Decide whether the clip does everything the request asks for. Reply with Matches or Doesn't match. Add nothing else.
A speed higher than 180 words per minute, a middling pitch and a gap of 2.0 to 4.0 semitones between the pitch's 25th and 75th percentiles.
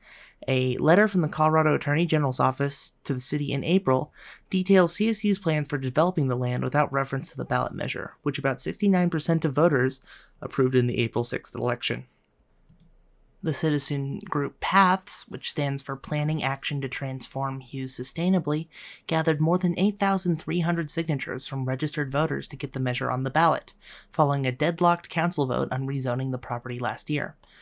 Doesn't match